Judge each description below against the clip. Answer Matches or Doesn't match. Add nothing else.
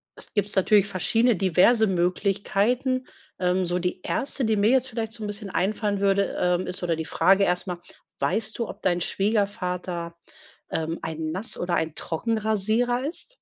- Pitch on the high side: Matches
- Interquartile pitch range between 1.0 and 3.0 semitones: Doesn't match